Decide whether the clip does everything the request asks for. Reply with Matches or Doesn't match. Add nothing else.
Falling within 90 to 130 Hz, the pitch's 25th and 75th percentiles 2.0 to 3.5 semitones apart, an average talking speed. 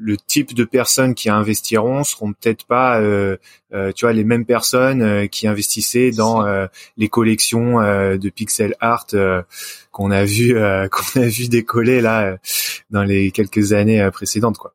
Matches